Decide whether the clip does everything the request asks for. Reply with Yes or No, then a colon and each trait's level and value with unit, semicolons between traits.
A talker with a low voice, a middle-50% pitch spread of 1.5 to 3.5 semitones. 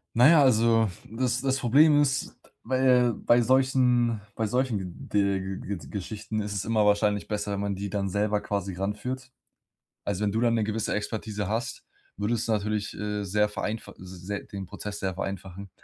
Yes: low, 105 Hz; average, 2.9 semitones